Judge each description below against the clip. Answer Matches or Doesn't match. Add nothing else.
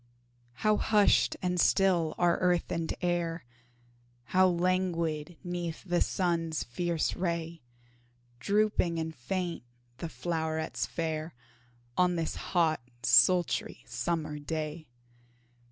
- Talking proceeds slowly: Matches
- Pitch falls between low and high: Matches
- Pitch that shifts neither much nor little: Doesn't match